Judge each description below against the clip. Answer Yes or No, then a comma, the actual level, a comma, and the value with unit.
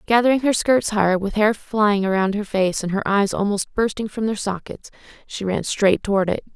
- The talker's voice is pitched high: Yes, high, 205 Hz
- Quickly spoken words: Yes, fast, 210 wpm